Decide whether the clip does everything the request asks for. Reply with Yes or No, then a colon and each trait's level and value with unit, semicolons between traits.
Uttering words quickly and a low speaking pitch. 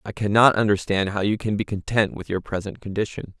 Yes: fast, 210 wpm; low, 100 Hz